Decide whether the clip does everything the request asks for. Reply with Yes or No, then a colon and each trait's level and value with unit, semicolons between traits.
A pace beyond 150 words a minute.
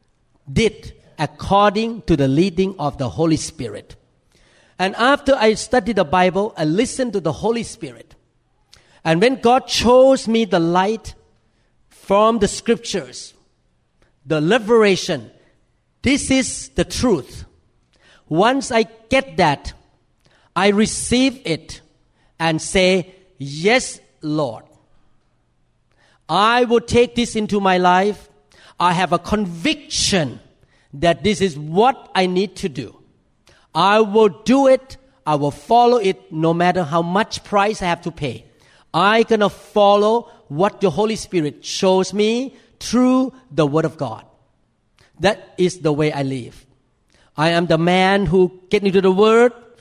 No: slow, 135 wpm